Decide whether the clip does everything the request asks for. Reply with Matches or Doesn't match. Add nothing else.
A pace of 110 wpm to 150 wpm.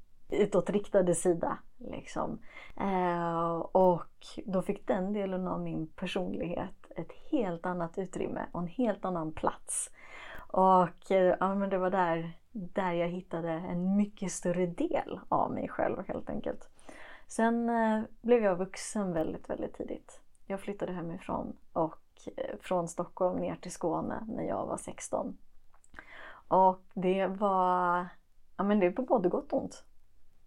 Matches